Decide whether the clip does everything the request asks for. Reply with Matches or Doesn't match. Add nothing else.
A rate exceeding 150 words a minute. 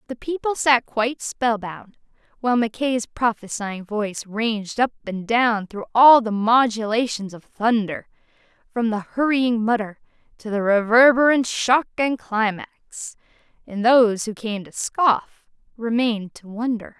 Doesn't match